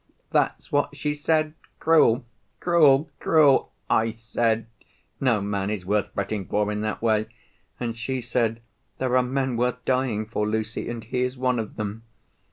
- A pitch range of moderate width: Yes, average, 3.4 semitones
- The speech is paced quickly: No, average, 165 wpm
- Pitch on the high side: No, low, 115 Hz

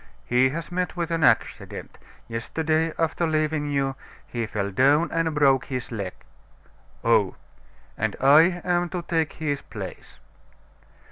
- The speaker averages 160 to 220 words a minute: No, slow, 135 wpm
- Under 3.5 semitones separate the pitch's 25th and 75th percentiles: No, average, 3.9 semitones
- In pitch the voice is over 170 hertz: No, medium, 155 Hz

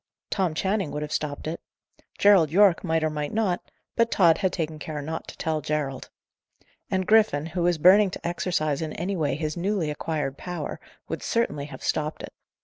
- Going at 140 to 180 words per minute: No, average, 190 wpm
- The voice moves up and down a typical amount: Yes, average, 3.7 semitones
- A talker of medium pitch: Yes, medium, 160 Hz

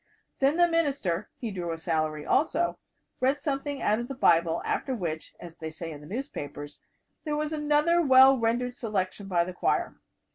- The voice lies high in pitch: Yes, high, 230 Hz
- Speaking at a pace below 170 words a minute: No, average, 180 wpm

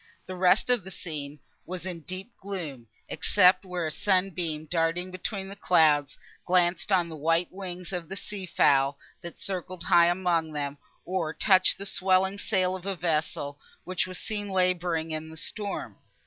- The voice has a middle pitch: Yes, medium, 180 Hz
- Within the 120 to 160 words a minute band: No, average, 170 wpm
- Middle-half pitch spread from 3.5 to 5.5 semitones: No, average, 2.7 semitones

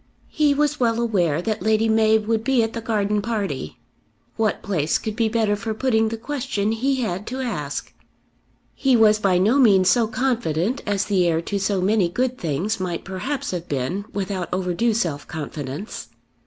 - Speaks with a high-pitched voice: Yes, high, 215 Hz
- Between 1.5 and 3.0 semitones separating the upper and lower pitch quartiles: No, average, 4.0 semitones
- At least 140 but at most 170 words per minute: No, average, 180 wpm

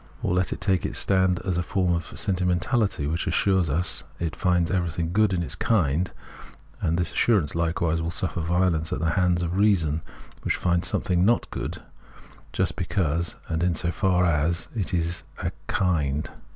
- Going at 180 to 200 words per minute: Yes, average, 185 wpm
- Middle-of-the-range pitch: No, very low, 85 Hz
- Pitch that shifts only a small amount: Yes, narrow, 2.0 semitones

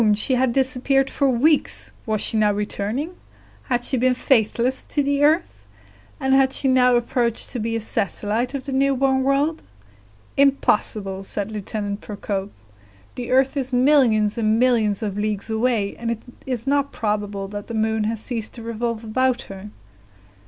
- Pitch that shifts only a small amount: No, average, 3.7 semitones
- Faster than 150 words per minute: Yes, average, 165 wpm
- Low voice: No, high, 235 Hz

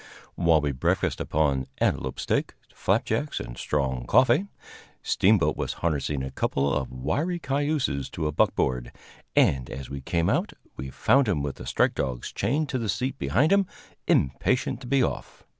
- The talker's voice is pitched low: Yes, very low, 75 Hz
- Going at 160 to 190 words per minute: Yes, average, 165 wpm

